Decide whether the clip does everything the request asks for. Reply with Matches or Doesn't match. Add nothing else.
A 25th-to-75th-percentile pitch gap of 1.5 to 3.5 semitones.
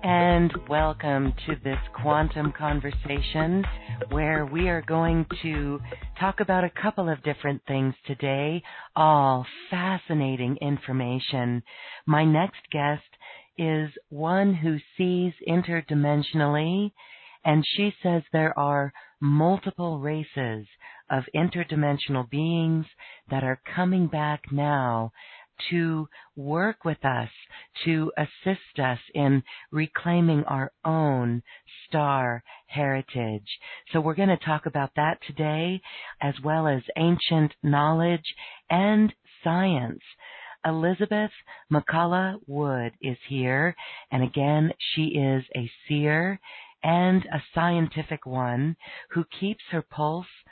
Matches